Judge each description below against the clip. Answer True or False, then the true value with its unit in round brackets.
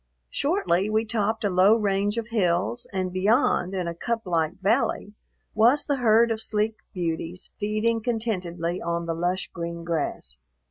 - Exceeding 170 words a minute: False (150 wpm)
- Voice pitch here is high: True (200 Hz)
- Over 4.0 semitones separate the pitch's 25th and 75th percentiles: True (4.4 semitones)